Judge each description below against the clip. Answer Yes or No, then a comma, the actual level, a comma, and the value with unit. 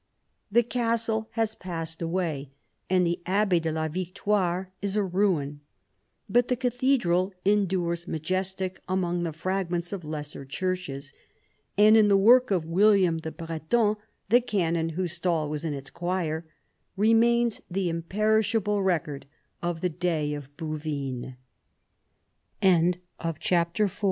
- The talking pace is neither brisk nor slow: No, slow, 110 wpm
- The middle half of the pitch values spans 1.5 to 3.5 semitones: No, average, 4.0 semitones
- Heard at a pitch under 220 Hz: Yes, medium, 185 Hz